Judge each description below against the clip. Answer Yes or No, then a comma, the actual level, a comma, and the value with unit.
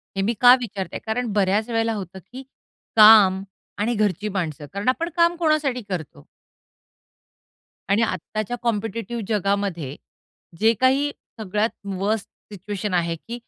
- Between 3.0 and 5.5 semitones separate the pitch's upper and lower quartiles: Yes, average, 3.7 semitones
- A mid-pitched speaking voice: No, high, 210 Hz